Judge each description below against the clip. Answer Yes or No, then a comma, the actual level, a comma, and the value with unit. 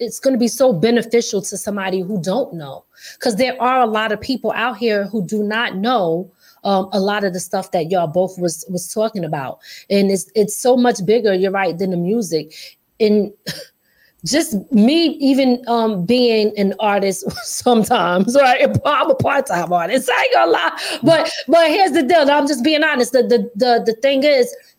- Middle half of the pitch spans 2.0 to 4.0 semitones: No, average, 4.6 semitones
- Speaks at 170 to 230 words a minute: Yes, average, 200 wpm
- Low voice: No, high, 220 Hz